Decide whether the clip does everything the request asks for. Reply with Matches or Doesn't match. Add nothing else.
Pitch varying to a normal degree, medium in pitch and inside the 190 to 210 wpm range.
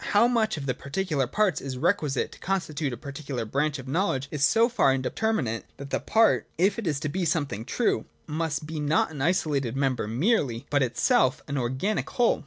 Doesn't match